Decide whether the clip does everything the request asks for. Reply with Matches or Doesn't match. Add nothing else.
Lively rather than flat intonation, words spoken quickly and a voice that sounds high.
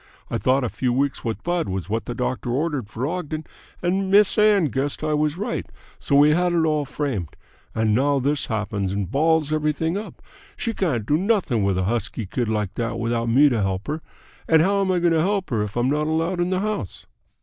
Doesn't match